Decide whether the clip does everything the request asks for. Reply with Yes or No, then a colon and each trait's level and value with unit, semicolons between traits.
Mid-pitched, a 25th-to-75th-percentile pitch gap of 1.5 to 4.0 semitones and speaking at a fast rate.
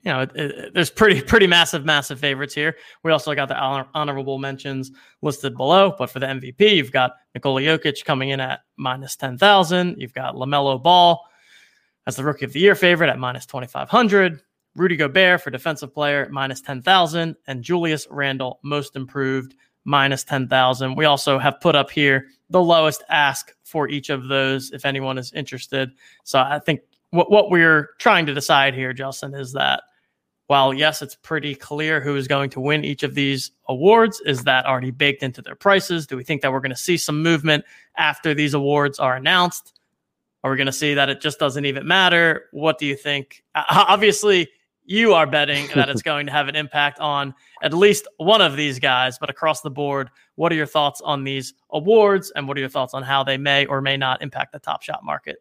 Yes: medium, 145 Hz; average, 3.1 semitones; fast, 210 wpm